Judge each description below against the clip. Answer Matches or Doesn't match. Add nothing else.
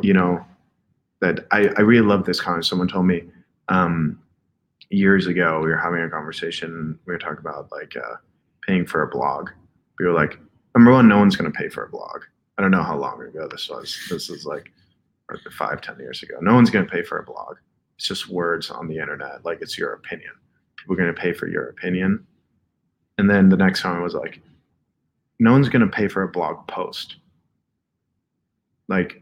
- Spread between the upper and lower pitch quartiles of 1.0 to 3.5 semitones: Matches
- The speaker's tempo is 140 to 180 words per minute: Doesn't match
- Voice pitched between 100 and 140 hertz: Doesn't match